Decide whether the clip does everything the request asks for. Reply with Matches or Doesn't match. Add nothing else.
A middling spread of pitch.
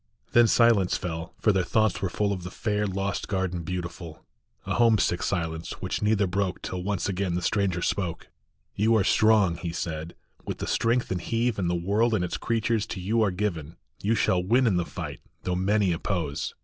Matches